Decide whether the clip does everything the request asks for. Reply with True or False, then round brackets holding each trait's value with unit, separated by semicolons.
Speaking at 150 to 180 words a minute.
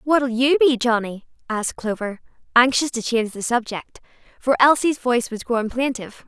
True (165 wpm)